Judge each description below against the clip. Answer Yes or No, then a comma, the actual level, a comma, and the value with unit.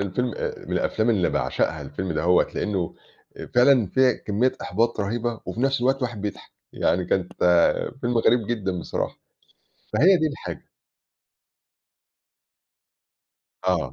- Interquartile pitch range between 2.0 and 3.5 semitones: No, average, 5.0 semitones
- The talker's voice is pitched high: No, low, 110 Hz